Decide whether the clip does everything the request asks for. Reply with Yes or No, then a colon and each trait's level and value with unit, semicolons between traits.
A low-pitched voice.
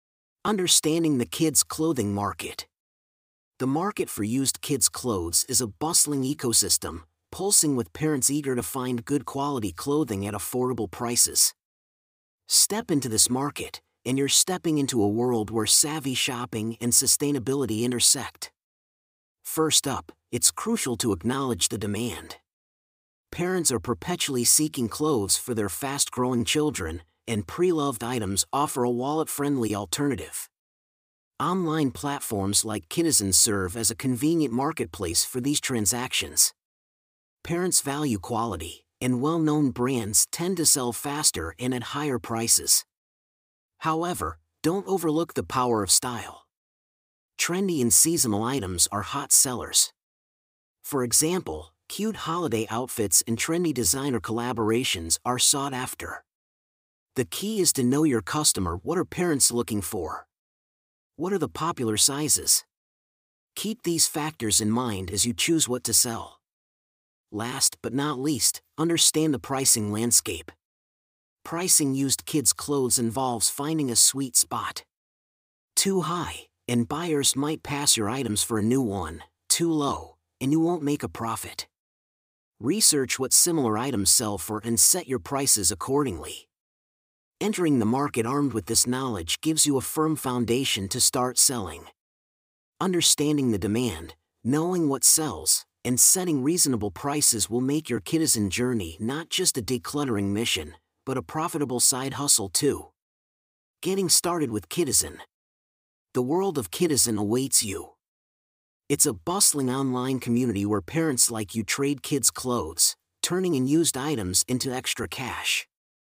Yes: low, 125 Hz